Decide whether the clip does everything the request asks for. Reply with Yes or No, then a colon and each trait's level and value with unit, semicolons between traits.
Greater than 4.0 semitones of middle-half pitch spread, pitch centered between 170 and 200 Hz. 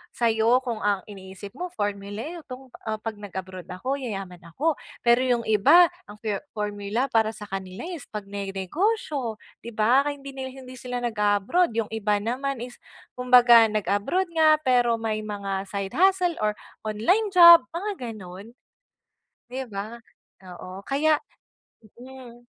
No: average, 4.5 semitones; high, 230 Hz